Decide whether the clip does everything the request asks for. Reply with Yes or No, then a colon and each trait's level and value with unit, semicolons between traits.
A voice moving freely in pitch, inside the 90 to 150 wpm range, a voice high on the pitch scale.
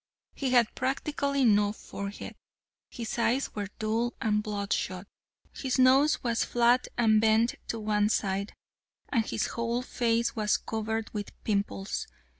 No: narrow, 2.5 semitones; slow, 135 wpm; high, 225 Hz